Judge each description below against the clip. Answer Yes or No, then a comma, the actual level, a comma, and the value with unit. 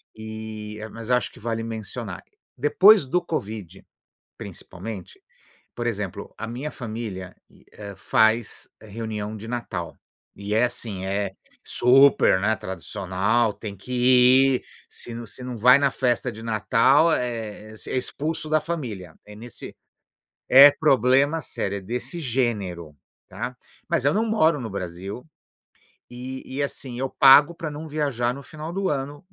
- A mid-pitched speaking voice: No, low, 115 Hz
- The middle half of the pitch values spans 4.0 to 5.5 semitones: Yes, average, 4.5 semitones